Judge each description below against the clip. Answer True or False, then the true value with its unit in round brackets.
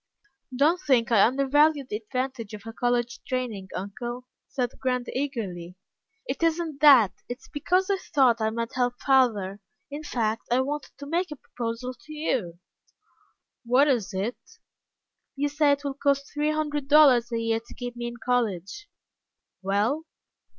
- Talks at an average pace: True (155 wpm)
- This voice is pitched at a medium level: False (250 Hz)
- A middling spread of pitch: True (4.1 semitones)